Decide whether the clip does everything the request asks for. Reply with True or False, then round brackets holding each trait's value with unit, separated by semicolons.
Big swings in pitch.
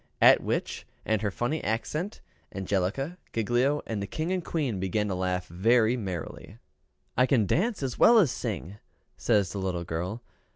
True (6.2 semitones)